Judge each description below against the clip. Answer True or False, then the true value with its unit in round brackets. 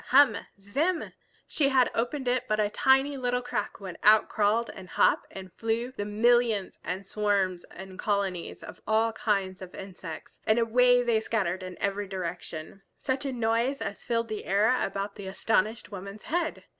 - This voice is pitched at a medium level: False (215 Hz)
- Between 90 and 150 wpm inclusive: False (170 wpm)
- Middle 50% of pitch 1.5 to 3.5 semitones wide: False (4.1 semitones)